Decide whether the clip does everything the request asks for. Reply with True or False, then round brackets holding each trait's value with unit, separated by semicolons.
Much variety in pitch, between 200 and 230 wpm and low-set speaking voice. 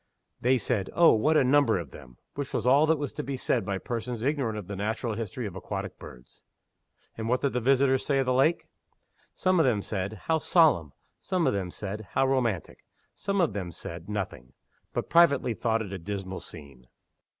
True (6.0 semitones; 205 wpm; 115 Hz)